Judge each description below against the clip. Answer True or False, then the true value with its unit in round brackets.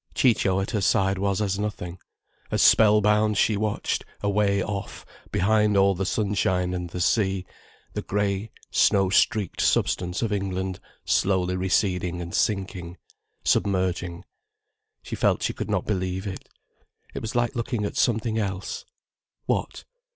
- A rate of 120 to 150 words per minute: True (145 wpm)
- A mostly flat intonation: True (2.3 semitones)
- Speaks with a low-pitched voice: True (100 Hz)